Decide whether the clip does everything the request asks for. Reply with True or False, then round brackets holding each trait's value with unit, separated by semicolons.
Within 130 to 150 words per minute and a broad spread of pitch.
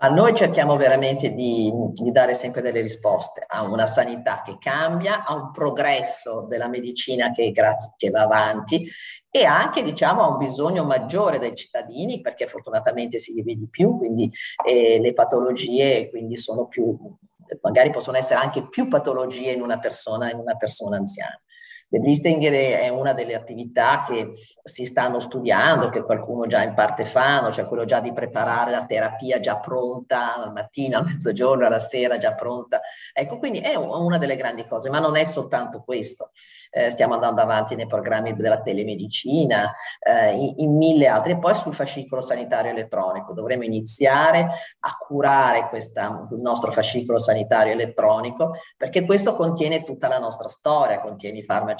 False (165 wpm; 7.8 semitones)